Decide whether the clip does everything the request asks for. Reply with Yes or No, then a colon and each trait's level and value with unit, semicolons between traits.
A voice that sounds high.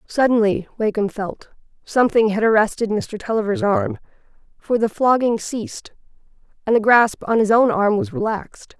Yes: high, 220 Hz